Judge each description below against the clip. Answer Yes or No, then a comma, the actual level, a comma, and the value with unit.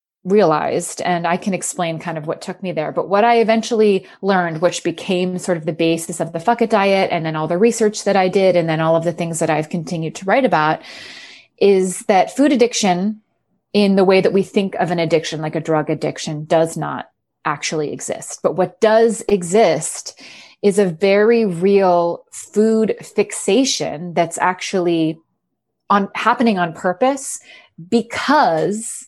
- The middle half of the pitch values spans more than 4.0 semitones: No, average, 3.7 semitones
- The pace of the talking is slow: No, average, 175 wpm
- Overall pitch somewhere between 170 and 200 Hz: Yes, medium, 185 Hz